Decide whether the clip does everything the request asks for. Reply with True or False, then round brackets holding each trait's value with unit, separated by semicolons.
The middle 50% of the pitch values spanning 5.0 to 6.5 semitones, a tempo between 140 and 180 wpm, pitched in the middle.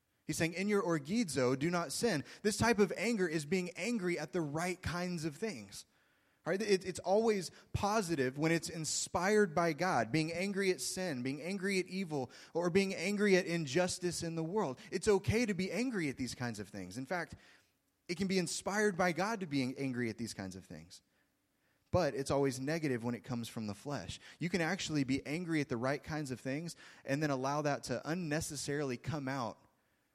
False (5.5 semitones; 205 wpm; 165 Hz)